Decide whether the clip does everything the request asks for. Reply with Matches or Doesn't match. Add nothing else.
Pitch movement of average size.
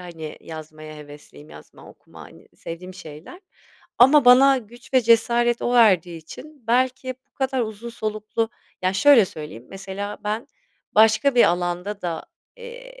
Doesn't match